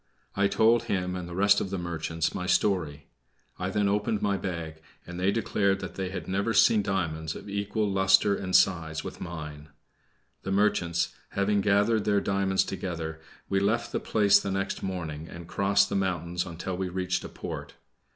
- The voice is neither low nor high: No, very low, 95 Hz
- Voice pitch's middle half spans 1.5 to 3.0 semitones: Yes, narrow, 2.6 semitones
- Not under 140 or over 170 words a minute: No, average, 180 wpm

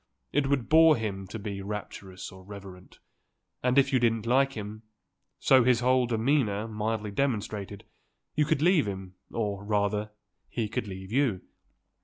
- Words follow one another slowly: No, average, 155 wpm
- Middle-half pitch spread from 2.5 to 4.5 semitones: Yes, average, 4.2 semitones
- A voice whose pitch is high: No, low, 110 Hz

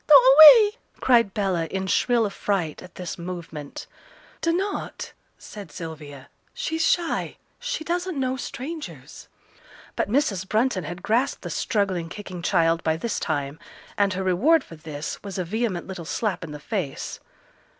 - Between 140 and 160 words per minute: Yes, average, 150 wpm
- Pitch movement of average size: No, wide, 7.7 semitones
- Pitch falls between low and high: No, high, 195 Hz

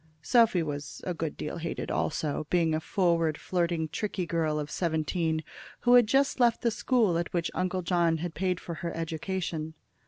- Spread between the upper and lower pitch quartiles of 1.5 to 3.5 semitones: Yes, average, 2.7 semitones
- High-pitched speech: No, medium, 170 Hz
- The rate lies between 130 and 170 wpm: No, average, 180 wpm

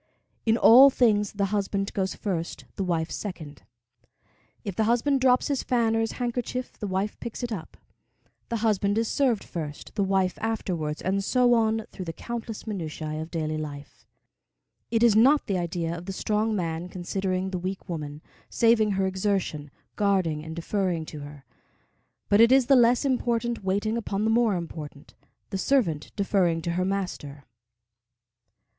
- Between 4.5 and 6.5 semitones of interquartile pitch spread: Yes, average, 4.9 semitones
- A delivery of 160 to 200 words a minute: Yes, average, 165 wpm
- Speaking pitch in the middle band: No, high, 195 Hz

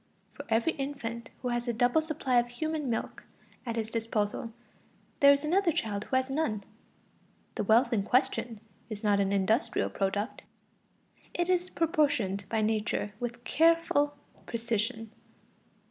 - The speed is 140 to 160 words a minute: Yes, average, 145 wpm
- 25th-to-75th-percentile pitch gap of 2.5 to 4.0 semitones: No, average, 4.7 semitones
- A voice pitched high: Yes, high, 240 Hz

